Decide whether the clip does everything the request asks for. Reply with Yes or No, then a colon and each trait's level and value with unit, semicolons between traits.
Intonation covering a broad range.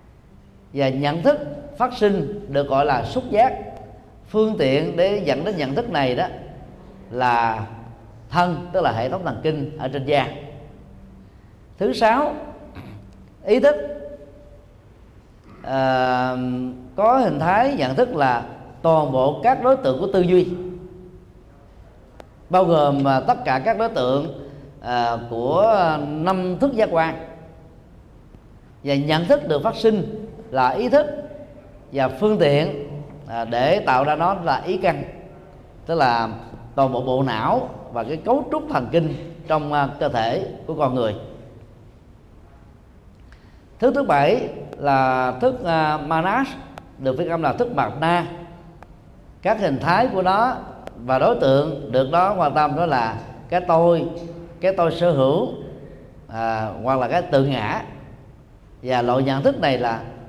Yes: wide, 6.5 semitones